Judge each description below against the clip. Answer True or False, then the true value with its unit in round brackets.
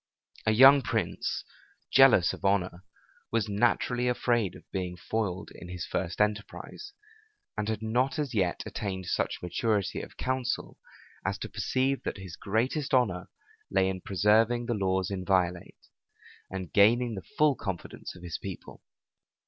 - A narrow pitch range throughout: False (4.5 semitones)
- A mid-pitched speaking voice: False (105 Hz)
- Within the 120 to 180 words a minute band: True (145 wpm)